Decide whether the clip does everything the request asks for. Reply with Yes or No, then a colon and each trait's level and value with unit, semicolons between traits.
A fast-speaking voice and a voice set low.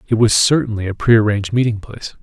No: average, 190 wpm; low, 110 Hz